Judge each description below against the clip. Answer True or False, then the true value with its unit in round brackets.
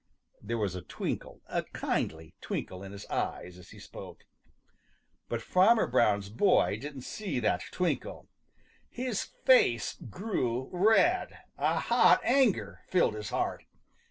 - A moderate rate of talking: False (130 wpm)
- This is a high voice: False (125 Hz)